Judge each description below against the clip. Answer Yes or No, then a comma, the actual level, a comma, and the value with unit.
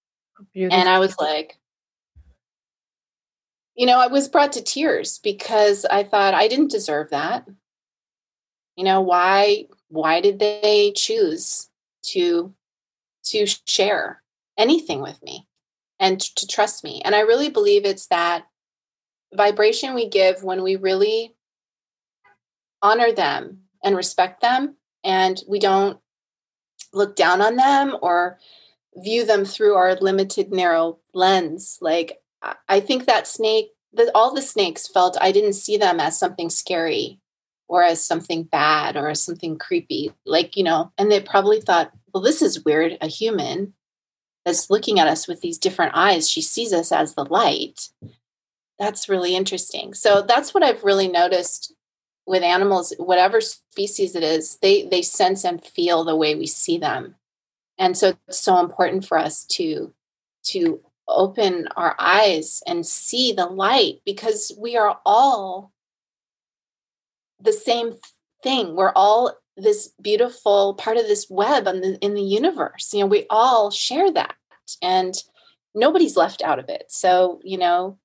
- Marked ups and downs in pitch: No, average, 5.0 semitones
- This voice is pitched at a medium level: No, high, 200 Hz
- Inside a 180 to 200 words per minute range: No, average, 150 wpm